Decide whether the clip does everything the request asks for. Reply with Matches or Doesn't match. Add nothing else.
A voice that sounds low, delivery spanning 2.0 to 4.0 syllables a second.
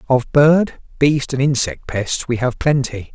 Matches